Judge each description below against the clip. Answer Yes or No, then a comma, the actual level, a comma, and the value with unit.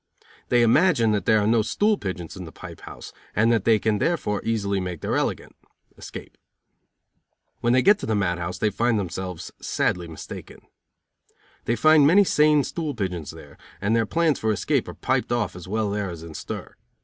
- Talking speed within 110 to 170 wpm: No, average, 195 wpm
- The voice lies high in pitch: No, low, 110 Hz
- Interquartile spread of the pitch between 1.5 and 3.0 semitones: No, average, 4.8 semitones